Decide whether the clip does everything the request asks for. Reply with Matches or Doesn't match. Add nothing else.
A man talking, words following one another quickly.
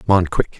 Matches